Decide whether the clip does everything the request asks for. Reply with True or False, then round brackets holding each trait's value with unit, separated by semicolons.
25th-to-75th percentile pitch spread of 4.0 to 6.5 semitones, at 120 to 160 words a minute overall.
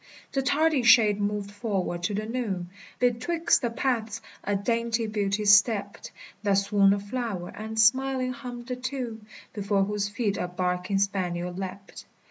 False (3.3 semitones; 150 wpm)